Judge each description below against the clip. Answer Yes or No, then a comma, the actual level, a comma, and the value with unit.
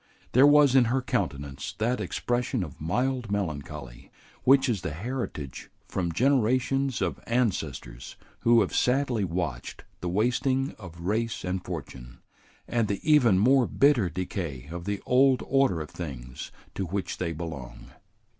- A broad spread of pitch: Yes, wide, 7.6 semitones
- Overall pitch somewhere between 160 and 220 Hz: No, low, 100 Hz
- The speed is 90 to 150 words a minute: Yes, average, 145 wpm